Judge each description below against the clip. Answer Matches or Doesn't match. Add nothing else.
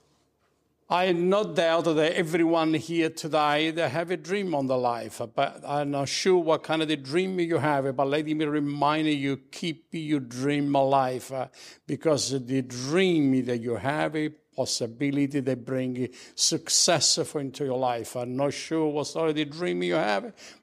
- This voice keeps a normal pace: Matches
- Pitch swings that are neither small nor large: Matches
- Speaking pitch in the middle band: Matches